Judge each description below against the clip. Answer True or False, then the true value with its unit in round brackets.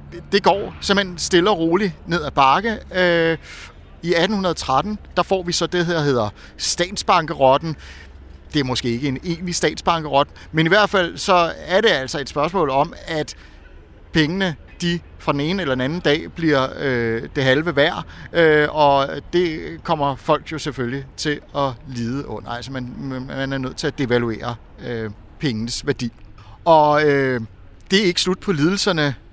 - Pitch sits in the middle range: True (145 Hz)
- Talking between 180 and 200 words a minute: False (170 wpm)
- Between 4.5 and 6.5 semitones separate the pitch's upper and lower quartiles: True (5.3 semitones)